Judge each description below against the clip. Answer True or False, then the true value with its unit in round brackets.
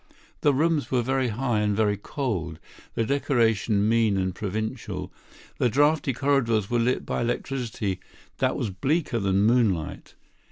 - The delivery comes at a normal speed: True (145 wpm)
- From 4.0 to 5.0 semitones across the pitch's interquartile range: True (4.5 semitones)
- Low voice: True (115 Hz)